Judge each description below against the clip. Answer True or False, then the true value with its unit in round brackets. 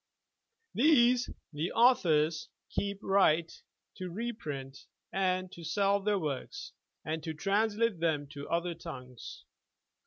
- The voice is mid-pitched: True (180 Hz)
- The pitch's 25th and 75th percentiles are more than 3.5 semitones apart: True (4.8 semitones)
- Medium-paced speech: False (125 wpm)